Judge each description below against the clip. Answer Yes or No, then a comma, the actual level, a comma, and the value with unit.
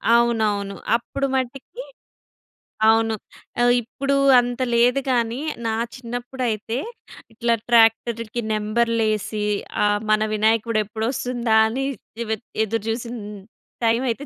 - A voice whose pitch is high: Yes, high, 230 Hz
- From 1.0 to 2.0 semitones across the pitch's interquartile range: Yes, narrow, 1.7 semitones